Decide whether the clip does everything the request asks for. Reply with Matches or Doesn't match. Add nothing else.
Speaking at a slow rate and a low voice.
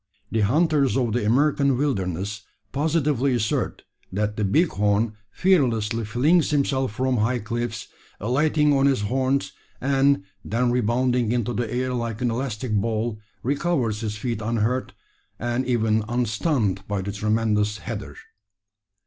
Matches